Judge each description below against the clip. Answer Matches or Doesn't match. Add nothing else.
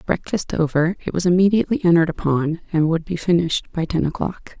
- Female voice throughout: Matches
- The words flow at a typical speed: Matches